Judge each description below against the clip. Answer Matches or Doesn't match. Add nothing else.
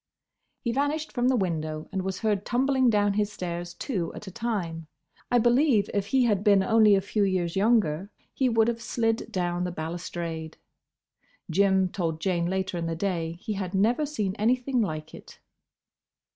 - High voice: Matches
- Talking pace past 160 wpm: Matches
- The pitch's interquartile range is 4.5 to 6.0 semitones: Matches